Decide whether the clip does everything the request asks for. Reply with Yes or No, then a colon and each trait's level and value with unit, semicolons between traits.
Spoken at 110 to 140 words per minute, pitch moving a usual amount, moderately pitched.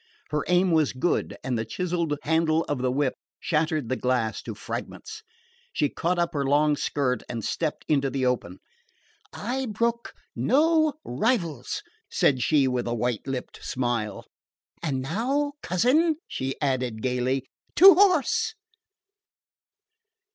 No: slow, 135 wpm; wide, 8.6 semitones; medium, 150 Hz